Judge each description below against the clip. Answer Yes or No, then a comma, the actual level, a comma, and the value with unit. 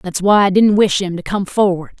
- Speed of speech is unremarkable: No, fast, 270 wpm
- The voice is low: No, high, 190 Hz